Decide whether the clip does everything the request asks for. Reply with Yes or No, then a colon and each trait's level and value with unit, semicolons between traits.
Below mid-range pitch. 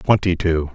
Yes: very low, 85 Hz